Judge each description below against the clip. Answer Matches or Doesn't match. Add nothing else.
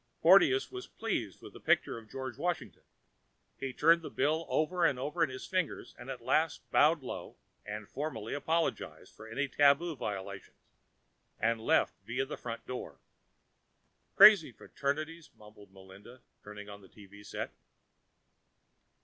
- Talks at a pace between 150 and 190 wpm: Doesn't match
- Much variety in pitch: Matches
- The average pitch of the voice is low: Matches